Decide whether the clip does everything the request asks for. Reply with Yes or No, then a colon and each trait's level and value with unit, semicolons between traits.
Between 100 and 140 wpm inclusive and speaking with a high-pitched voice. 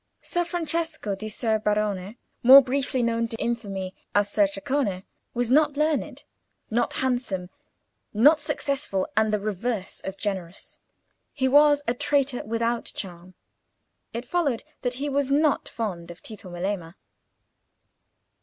Yes: slow, 135 wpm; high, 235 Hz